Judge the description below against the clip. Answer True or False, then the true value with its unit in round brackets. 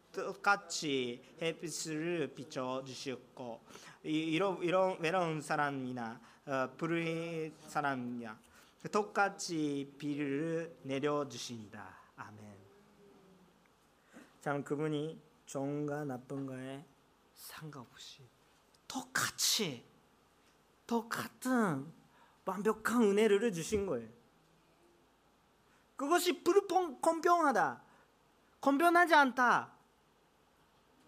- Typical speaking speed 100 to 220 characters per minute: True (170 characters per minute)